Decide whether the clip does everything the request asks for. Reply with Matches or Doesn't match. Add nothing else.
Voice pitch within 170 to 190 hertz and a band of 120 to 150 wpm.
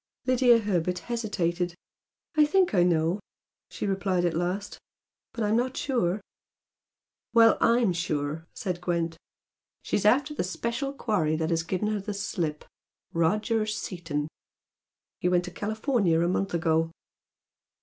Matches